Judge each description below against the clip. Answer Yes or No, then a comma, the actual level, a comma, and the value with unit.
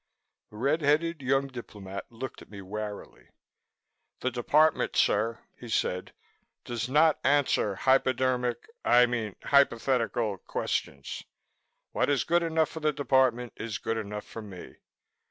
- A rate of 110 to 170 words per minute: Yes, slow, 135 wpm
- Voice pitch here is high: No, low, 125 Hz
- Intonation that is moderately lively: Yes, average, 4.5 semitones